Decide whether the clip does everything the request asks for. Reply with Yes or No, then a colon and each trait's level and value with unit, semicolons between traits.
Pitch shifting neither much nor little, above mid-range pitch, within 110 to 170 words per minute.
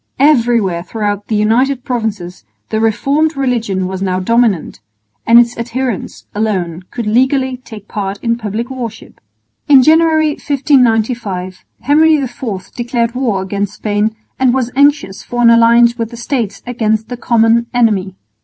Yes: average, 3.5 semitones; high, 230 Hz; average, 145 wpm